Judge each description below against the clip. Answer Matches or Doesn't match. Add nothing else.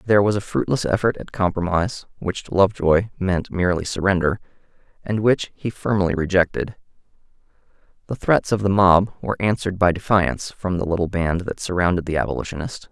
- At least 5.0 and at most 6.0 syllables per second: Matches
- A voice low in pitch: Matches